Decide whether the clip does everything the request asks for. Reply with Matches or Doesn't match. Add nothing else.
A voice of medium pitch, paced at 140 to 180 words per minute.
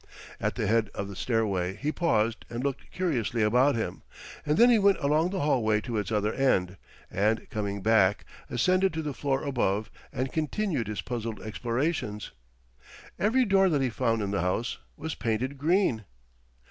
Doesn't match